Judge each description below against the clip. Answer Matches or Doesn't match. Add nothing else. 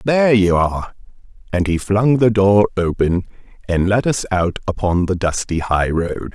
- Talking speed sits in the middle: Matches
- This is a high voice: Doesn't match